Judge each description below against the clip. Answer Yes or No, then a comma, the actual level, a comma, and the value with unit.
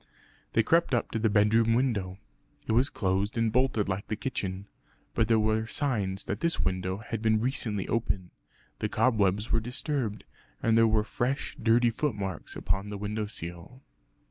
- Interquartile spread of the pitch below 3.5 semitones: Yes, average, 2.9 semitones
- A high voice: No, low, 110 Hz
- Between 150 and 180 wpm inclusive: Yes, average, 170 wpm